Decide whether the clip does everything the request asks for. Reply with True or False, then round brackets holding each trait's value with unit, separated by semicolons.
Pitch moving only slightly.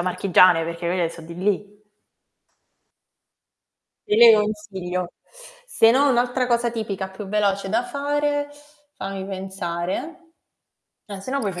False (4.4 semitones)